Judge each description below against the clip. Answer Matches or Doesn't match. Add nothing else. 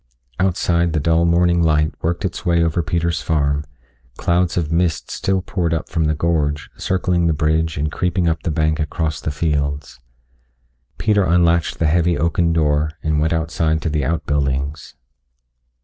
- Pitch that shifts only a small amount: Matches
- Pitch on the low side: Matches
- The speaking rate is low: Doesn't match